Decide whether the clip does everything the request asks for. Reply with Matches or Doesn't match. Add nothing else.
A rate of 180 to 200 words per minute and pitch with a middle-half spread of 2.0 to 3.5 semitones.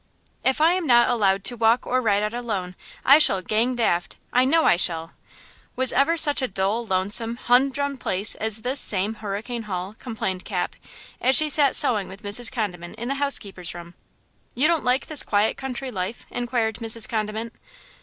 Doesn't match